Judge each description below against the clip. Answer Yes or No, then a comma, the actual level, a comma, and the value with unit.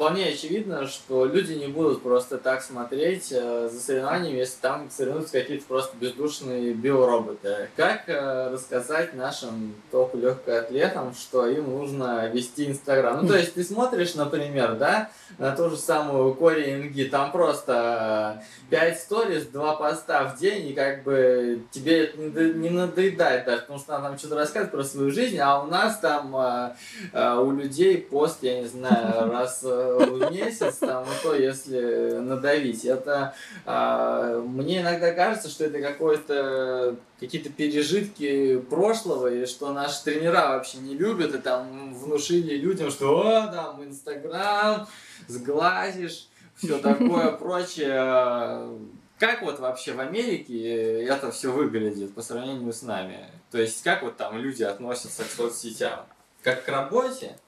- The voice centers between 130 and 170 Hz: Yes, medium, 140 Hz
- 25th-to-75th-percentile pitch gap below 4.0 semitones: No, average, 4.3 semitones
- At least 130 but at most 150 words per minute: Yes, average, 145 wpm